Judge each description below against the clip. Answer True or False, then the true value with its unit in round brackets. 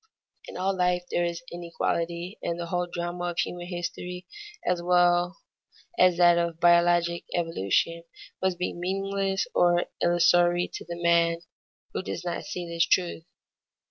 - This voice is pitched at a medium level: True (175 Hz)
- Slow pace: False (145 wpm)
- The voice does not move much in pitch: True (0.8 semitones)